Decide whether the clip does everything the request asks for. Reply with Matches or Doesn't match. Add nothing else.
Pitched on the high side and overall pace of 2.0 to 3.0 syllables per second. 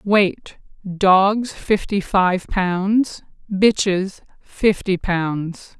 Matches